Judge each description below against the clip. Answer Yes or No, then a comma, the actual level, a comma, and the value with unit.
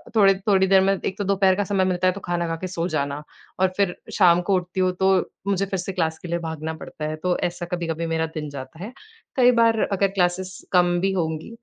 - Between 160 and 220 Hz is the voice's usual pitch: Yes, medium, 185 Hz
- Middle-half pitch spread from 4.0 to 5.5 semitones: No, narrow, 2.4 semitones